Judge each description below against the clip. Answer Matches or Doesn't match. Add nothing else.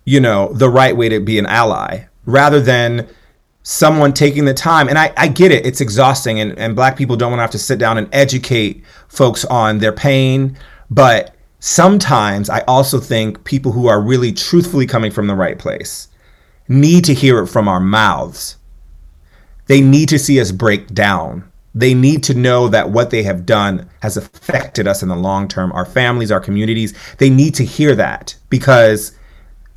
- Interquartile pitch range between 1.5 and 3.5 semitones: Doesn't match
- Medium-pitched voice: Doesn't match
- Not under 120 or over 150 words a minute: Doesn't match